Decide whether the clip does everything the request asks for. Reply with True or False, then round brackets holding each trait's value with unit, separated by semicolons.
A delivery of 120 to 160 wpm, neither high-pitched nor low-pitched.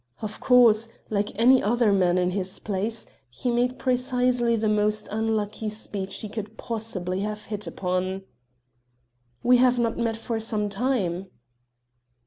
False (140 wpm; 215 Hz)